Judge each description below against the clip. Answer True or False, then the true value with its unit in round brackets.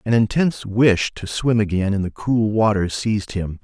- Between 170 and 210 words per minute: True (200 wpm)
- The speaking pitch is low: True (105 Hz)